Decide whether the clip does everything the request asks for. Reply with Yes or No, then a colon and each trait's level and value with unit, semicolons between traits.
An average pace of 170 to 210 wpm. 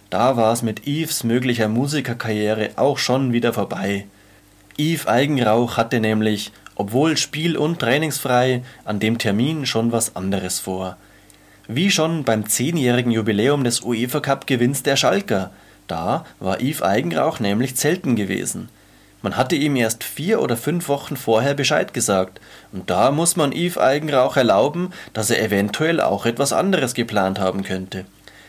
No: average, 145 wpm